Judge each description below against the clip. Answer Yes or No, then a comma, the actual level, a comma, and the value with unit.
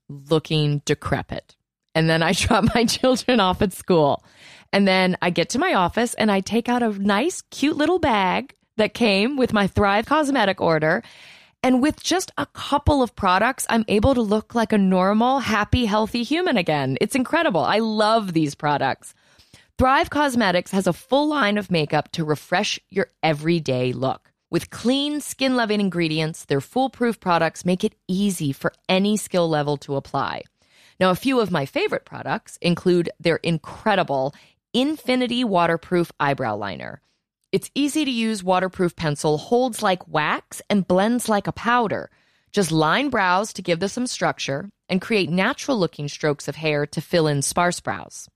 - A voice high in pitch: Yes, high, 195 Hz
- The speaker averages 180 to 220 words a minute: No, average, 170 wpm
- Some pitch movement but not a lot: No, wide, 6.4 semitones